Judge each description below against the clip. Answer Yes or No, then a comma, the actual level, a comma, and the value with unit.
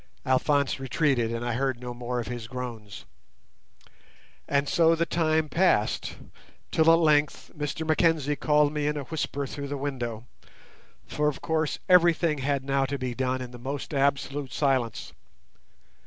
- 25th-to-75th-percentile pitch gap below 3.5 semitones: Yes, average, 3.1 semitones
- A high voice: No, medium, 140 Hz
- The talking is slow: No, average, 155 wpm